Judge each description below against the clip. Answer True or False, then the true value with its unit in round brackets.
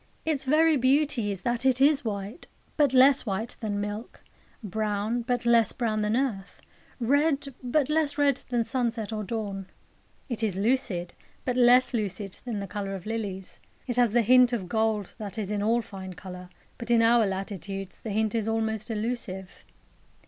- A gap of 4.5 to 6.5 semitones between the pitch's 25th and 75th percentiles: False (3.6 semitones)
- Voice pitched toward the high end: True (225 Hz)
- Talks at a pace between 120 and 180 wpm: True (175 wpm)